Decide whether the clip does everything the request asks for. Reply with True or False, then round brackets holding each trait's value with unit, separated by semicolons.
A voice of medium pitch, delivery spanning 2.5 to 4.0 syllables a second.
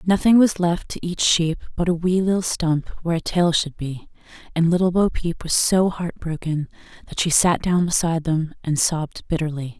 False (170 Hz; 5.1 syllables/s)